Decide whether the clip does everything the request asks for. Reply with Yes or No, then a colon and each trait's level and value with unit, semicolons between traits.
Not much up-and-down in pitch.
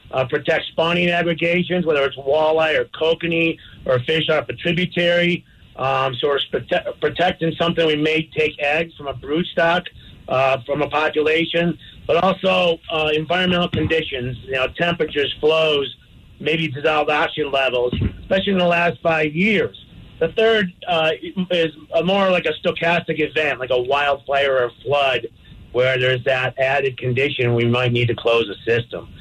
No: average, 4.0 semitones